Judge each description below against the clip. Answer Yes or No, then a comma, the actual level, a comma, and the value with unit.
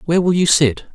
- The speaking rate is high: Yes, fast, 255 wpm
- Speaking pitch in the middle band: Yes, medium, 160 Hz